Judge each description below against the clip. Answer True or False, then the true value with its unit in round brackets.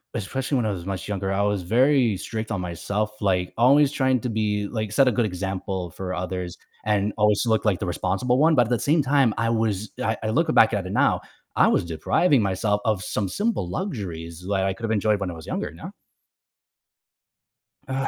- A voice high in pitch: False (105 Hz)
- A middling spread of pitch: True (4.4 semitones)